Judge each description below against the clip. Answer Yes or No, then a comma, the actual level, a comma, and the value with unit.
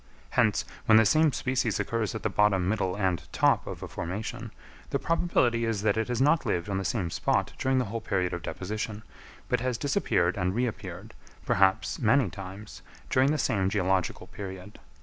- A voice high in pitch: No, low, 105 Hz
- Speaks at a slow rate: No, average, 185 wpm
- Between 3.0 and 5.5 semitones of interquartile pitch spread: Yes, average, 4.1 semitones